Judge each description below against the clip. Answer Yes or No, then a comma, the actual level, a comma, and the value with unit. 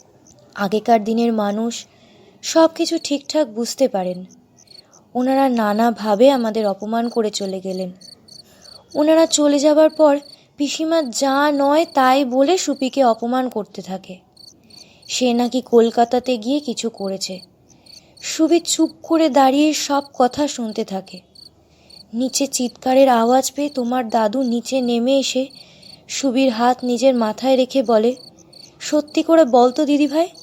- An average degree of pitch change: Yes, average, 4.2 semitones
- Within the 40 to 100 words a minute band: No, fast, 120 wpm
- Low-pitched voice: No, very high, 255 Hz